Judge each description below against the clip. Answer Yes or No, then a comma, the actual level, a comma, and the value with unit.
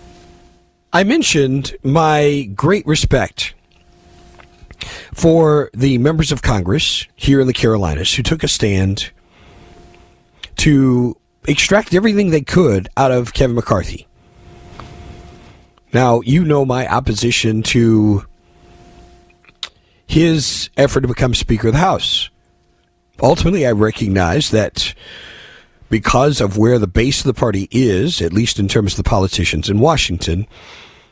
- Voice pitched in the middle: No, low, 115 Hz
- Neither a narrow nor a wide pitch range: No, wide, 6.4 semitones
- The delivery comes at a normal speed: No, slow, 120 wpm